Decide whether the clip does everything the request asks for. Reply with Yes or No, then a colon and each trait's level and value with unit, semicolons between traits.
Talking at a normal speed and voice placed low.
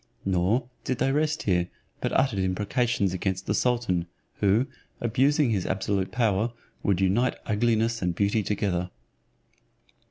No: slow, 130 wpm; low, 105 Hz